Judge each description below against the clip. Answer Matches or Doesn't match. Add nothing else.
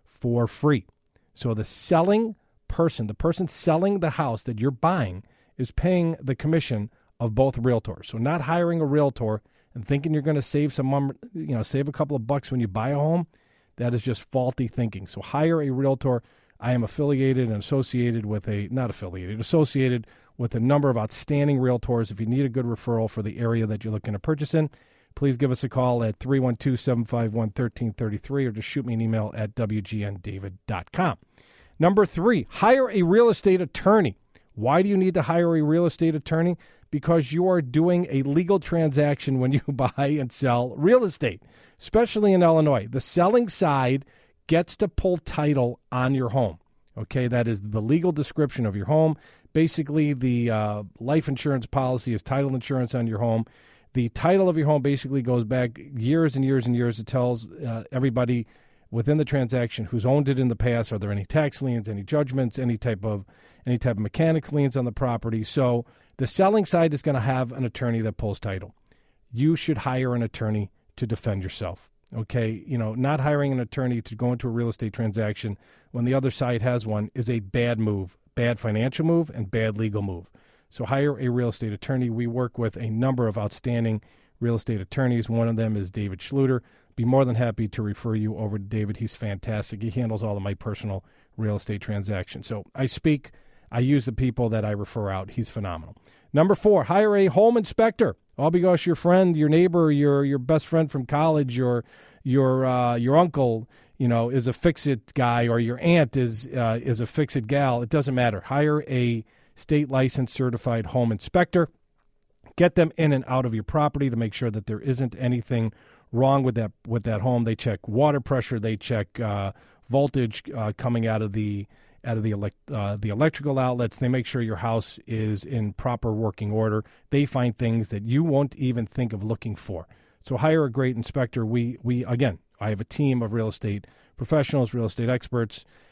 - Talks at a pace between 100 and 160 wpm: Doesn't match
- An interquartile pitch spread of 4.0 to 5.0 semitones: Matches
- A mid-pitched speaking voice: Doesn't match